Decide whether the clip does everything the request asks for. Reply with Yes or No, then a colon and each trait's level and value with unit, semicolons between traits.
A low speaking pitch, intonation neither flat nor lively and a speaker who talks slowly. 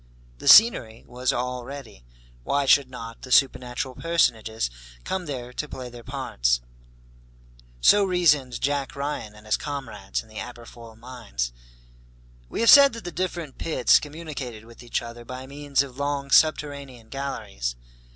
No: low, 130 Hz; average, 3.7 semitones; average, 150 wpm